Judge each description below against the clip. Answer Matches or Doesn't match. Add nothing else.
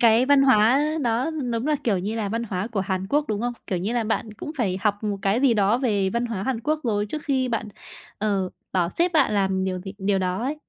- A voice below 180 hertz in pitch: Doesn't match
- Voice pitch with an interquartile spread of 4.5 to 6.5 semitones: Doesn't match